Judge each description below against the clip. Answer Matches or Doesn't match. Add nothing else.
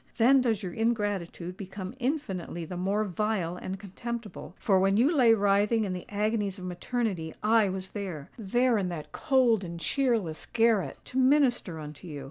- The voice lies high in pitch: Matches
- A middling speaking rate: Matches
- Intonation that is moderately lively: Matches